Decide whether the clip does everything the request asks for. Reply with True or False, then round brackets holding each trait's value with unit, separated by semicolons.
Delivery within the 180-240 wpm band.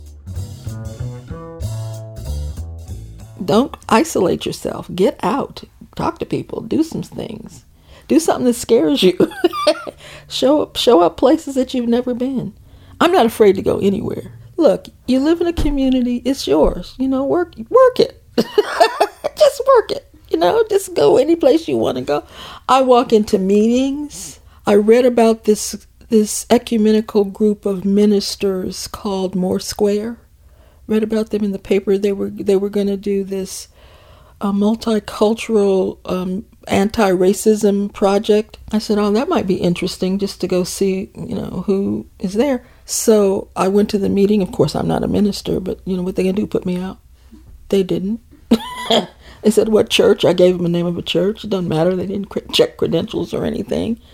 False (170 wpm)